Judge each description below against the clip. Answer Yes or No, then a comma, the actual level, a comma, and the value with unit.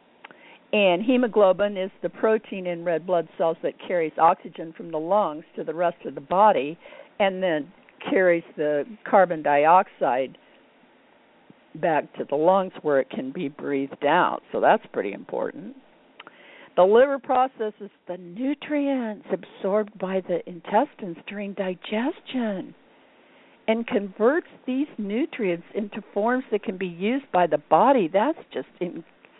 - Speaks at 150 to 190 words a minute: No, average, 140 wpm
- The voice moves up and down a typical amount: No, wide, 6.1 semitones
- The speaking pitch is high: Yes, high, 205 Hz